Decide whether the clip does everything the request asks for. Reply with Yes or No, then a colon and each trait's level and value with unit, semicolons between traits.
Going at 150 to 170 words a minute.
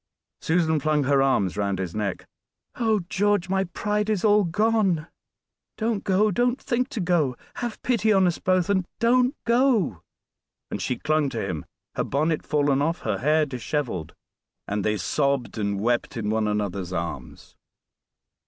Yes: average, 160 wpm